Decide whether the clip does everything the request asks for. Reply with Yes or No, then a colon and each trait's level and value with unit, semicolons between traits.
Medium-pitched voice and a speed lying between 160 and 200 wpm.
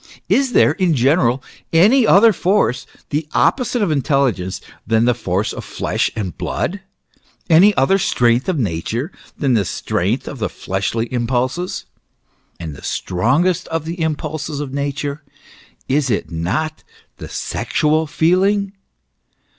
No: medium, 145 Hz; slow, 135 wpm